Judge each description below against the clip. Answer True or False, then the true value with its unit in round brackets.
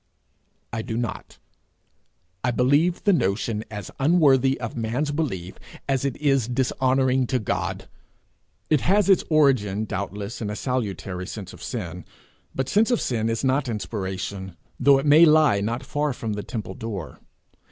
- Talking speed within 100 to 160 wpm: True (155 wpm)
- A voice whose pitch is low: True (120 Hz)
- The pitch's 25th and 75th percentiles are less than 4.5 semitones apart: False (5.1 semitones)